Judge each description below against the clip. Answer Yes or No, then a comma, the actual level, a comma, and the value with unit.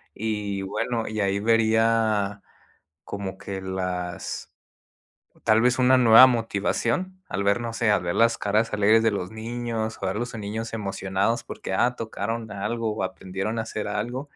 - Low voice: Yes, low, 110 Hz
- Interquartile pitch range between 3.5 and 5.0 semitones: No, narrow, 2.4 semitones